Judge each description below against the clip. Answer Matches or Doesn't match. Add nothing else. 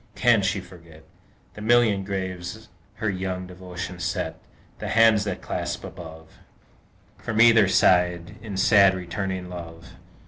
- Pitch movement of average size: Matches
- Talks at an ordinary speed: Doesn't match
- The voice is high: Doesn't match